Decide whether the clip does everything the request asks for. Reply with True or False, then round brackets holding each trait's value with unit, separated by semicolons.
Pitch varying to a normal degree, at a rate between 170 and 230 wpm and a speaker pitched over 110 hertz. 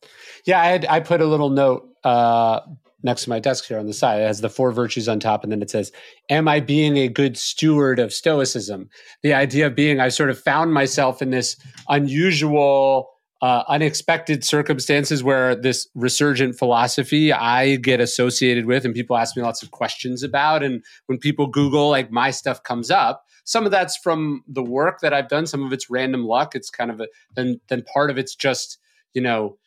True (3.2 semitones; 205 wpm; 135 Hz)